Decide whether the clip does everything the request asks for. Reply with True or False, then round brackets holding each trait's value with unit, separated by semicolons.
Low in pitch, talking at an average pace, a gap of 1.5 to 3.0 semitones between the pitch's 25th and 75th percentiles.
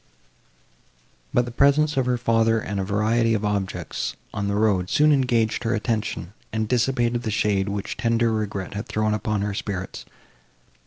True (110 Hz; 165 wpm; 2.7 semitones)